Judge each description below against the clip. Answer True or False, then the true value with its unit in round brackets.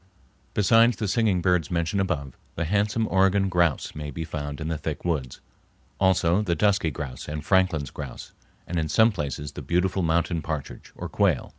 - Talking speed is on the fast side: False (175 wpm)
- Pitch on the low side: True (85 Hz)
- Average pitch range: True (4.1 semitones)